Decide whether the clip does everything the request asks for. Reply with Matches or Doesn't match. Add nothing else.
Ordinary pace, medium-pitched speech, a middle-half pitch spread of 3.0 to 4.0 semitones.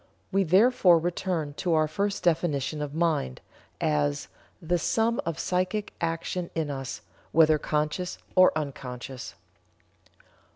Doesn't match